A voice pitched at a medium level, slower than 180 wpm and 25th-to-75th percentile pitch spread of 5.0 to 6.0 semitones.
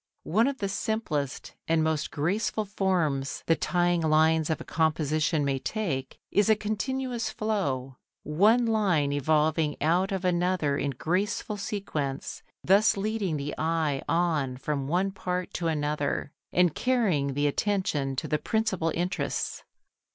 Yes: medium, 165 Hz; average, 140 wpm; average, 5.3 semitones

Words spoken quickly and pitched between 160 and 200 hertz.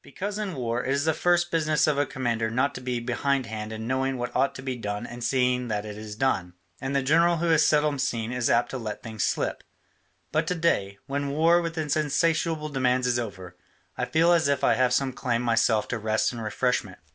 No: fast, 225 wpm; low, 130 Hz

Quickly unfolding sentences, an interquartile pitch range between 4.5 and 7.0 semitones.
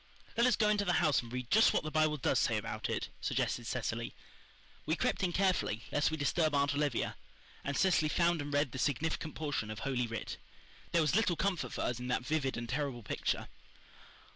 Yes: fast, 210 wpm; average, 4.8 semitones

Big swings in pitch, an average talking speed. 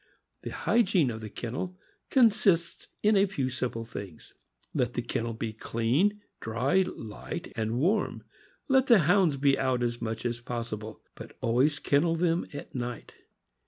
Yes: wide, 7.4 semitones; average, 160 wpm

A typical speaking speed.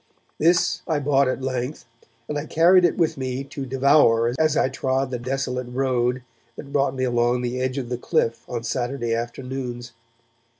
Yes: average, 175 wpm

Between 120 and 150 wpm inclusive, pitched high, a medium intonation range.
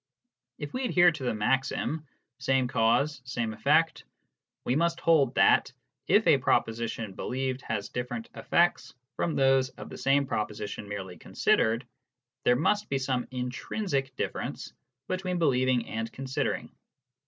No: average, 140 wpm; low, 130 Hz; average, 4.7 semitones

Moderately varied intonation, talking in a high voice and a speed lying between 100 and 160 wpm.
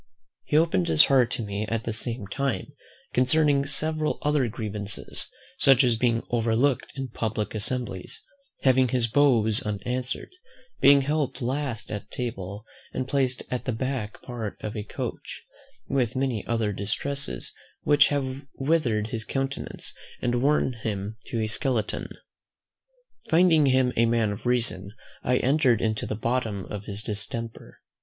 No: average, 3.8 semitones; low, 120 Hz; average, 145 wpm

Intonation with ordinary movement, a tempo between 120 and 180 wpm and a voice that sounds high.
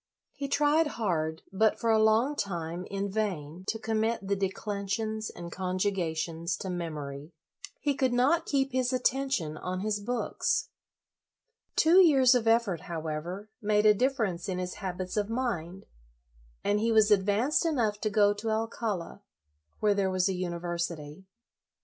Yes: average, 4.2 semitones; average, 155 wpm; high, 205 Hz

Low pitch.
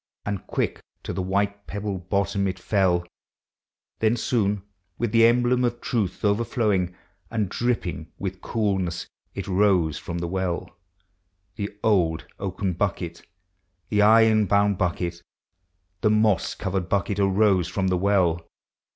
Yes: low, 100 Hz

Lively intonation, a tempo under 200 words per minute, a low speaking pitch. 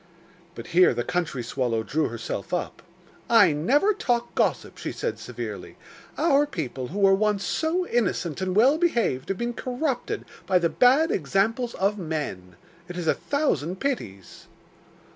No: wide, 8.1 semitones; average, 155 wpm; high, 195 Hz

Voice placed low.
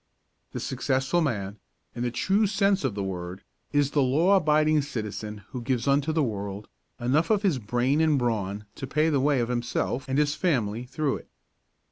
Yes: low, 130 Hz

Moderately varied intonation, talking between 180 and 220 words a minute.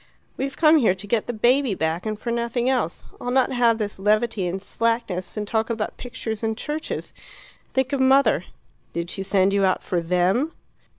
Yes: average, 4.4 semitones; average, 190 wpm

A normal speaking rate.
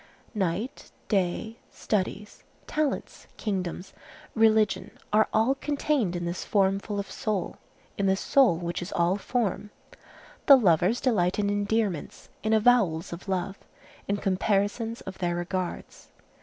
No: slow, 130 wpm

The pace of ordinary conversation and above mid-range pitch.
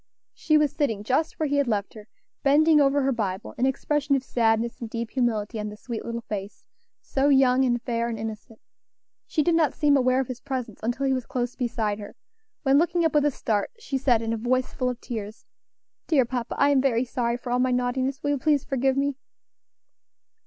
No: fast, 215 wpm; very high, 255 Hz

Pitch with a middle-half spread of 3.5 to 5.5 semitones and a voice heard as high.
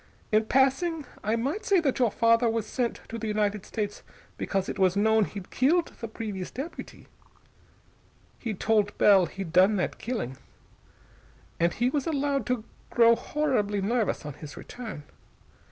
Yes: average, 4.2 semitones; high, 225 Hz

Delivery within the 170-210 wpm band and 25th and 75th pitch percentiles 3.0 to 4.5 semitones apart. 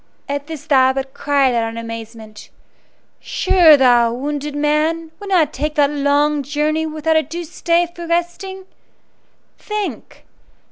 No: average, 140 wpm; average, 3.6 semitones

